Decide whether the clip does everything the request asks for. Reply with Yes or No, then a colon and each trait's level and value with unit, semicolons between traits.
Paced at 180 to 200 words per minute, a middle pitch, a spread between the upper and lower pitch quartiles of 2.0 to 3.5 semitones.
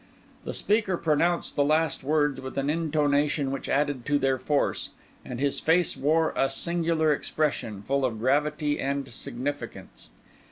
No: average, 150 wpm; medium, 145 Hz; narrow, 2.5 semitones